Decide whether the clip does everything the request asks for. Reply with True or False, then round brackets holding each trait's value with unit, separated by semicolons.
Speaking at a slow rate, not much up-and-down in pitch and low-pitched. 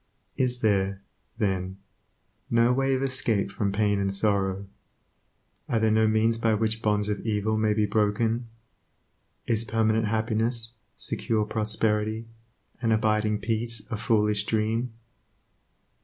True (125 wpm; 1.4 semitones; 110 Hz)